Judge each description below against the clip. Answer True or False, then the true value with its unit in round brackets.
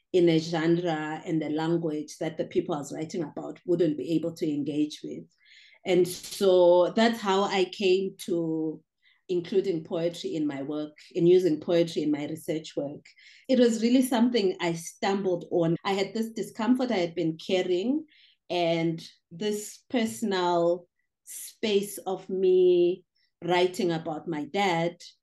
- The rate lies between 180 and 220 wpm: False (150 wpm)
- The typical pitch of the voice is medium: True (175 Hz)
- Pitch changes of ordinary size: True (3.3 semitones)